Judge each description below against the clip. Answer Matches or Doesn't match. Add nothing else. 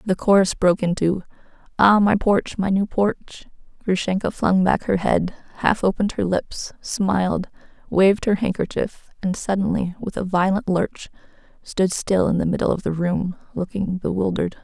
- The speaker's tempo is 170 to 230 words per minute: Doesn't match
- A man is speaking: Doesn't match